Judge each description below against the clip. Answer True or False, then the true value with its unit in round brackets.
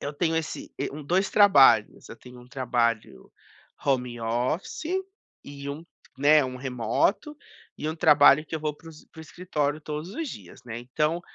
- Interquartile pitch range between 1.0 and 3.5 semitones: False (4.2 semitones)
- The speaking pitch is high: False (145 Hz)